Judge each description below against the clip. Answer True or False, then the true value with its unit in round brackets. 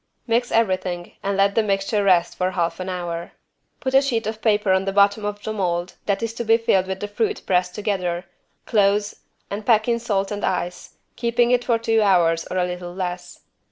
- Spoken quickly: True (210 wpm)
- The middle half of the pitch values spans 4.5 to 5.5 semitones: False (3.5 semitones)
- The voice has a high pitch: True (200 Hz)